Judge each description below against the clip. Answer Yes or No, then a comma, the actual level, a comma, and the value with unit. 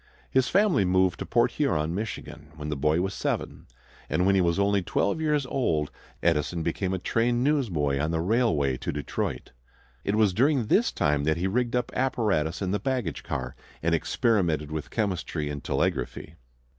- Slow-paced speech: No, average, 180 wpm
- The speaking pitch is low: Yes, very low, 95 Hz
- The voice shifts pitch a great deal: Yes, wide, 7.1 semitones